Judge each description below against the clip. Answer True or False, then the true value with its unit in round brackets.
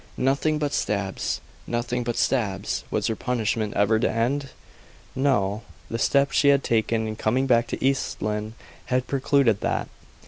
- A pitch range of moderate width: True (3.9 semitones)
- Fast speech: False (160 wpm)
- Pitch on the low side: True (120 Hz)